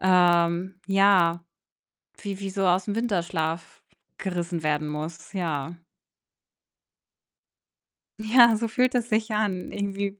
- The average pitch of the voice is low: No, high, 190 Hz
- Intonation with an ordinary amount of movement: Yes, average, 3.2 semitones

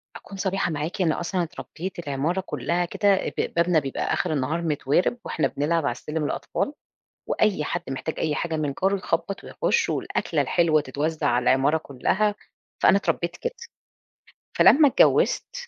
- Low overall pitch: No, medium, 165 Hz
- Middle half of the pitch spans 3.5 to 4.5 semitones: Yes, average, 4.0 semitones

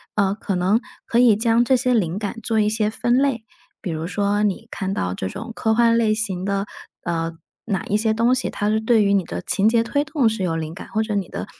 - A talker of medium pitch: No, high, 215 Hz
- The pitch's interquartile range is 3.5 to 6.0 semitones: No, average, 3.0 semitones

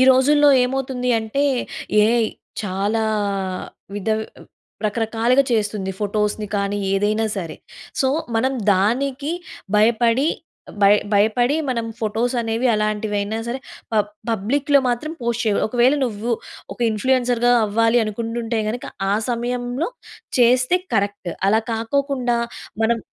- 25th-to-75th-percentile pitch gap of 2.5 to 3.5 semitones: Yes, average, 2.9 semitones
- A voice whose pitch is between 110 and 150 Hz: No, high, 230 Hz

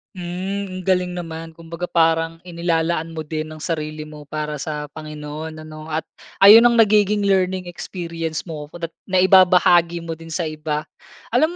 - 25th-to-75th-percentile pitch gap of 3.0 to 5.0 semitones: No, narrow, 2.5 semitones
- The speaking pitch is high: No, medium, 165 Hz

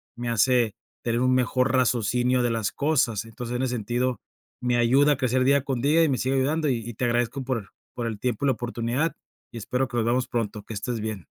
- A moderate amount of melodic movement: No, narrow, 1.9 semitones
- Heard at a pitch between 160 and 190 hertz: No, low, 125 Hz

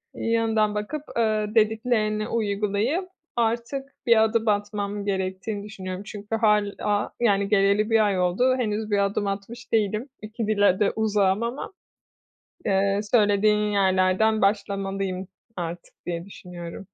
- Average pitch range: No, narrow, 2.0 semitones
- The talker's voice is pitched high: Yes, high, 210 Hz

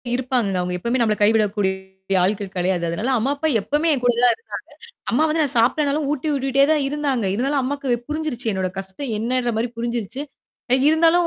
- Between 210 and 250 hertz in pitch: Yes, high, 245 Hz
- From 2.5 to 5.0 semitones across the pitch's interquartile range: No, wide, 5.6 semitones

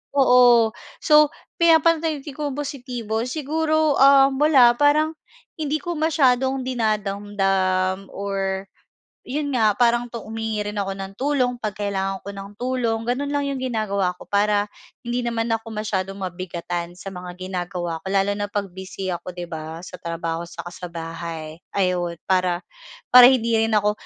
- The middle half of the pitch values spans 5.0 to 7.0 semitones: Yes, wide, 5.6 semitones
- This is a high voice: Yes, high, 210 Hz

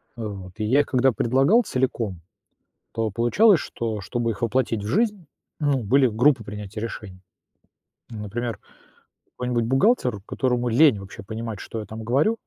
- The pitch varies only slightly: No, average, 3.8 semitones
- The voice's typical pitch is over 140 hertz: No, low, 115 Hz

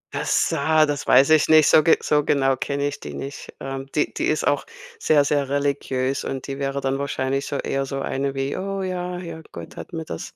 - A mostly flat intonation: Yes, narrow, 2.3 semitones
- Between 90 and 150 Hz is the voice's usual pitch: Yes, medium, 140 Hz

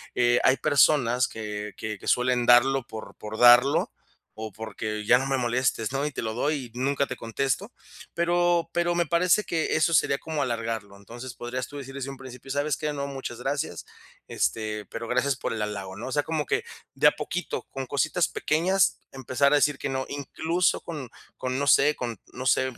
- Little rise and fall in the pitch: No, average, 3.7 semitones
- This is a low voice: Yes, low, 130 Hz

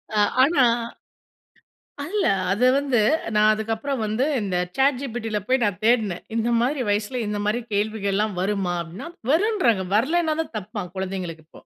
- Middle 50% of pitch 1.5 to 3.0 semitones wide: No, average, 4.5 semitones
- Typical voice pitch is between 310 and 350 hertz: No, high, 220 Hz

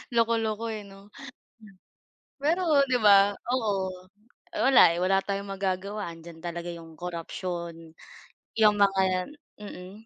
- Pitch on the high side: Yes, high, 195 Hz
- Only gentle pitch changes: No, average, 3.4 semitones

